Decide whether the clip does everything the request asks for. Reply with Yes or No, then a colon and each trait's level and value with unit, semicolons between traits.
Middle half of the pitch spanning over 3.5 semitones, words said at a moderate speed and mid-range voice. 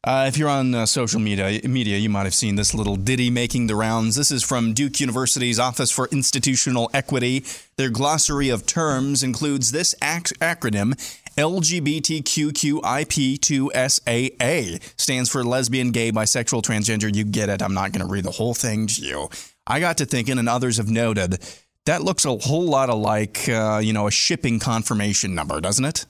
No: average, 4.1 semitones; average, 180 wpm; low, 125 Hz